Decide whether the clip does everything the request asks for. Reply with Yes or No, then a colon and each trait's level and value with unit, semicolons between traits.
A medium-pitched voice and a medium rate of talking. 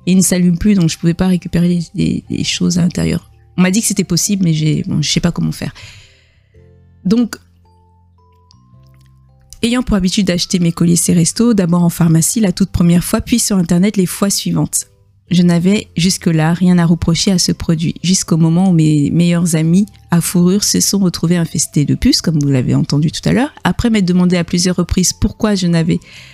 Yes: medium, 175 Hz; average, 205 wpm